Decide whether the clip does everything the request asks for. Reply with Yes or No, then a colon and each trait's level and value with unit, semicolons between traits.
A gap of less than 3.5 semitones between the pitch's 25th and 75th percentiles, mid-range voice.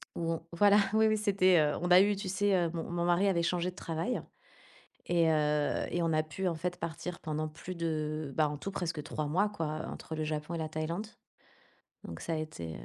Yes: average, 2.8 semitones; medium, 165 Hz